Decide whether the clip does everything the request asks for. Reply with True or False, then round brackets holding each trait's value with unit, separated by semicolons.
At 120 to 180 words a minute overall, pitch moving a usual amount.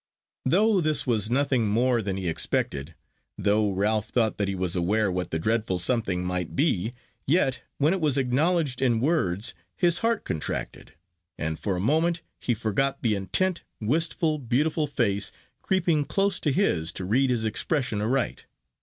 False (165 wpm; 7.4 semitones)